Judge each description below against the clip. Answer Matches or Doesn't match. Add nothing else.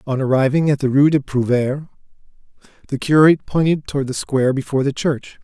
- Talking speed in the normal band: Matches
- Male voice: Matches